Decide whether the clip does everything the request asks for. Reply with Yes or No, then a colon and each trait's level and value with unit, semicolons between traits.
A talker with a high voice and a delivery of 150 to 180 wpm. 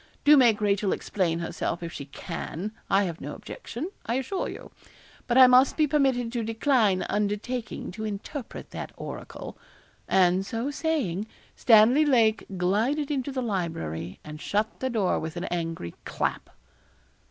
Yes: high, 220 Hz; average, 155 wpm